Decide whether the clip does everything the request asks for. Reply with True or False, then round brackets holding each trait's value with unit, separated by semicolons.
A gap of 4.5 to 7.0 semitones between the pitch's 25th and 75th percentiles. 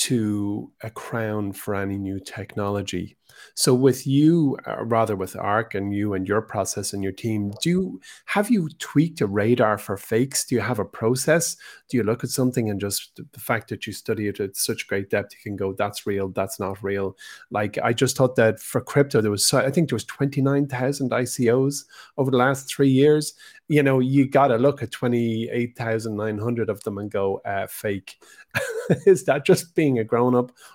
True (4.9 semitones)